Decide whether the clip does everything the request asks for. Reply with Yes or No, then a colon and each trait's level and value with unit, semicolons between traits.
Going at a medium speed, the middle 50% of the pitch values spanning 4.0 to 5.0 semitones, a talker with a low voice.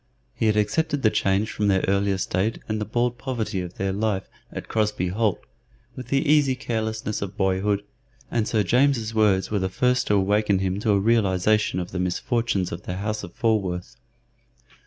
No: average, 185 wpm; average, 2.9 semitones; low, 105 Hz